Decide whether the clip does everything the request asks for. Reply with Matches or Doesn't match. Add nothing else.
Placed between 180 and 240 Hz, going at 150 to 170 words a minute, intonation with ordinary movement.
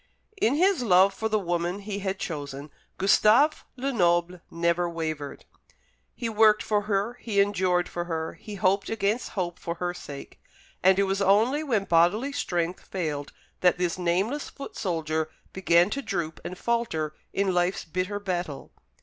Matches